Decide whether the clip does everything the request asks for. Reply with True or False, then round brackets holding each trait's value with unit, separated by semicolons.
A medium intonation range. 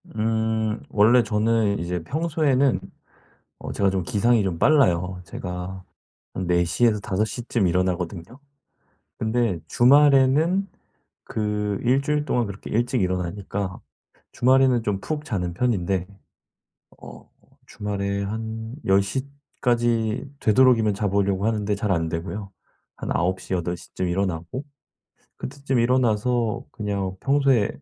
True (4.6 semitones)